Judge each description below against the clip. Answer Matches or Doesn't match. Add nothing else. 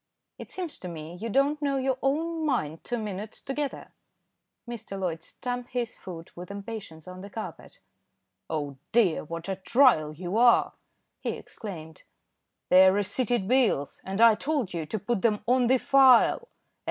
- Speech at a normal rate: Matches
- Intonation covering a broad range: Matches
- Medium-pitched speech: Doesn't match